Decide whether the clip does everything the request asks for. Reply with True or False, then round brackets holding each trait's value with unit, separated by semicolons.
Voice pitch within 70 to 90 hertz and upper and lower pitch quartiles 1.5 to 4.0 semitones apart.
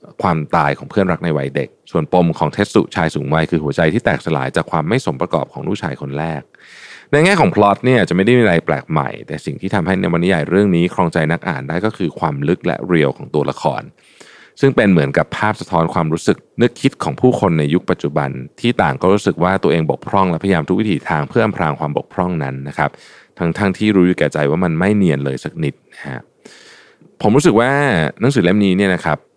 False (85 Hz; 4.9 semitones)